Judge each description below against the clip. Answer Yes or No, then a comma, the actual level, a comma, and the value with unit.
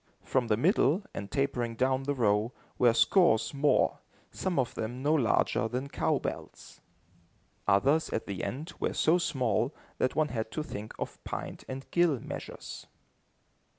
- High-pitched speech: No, low, 130 Hz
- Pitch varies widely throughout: No, average, 4.8 semitones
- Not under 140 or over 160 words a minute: Yes, average, 155 wpm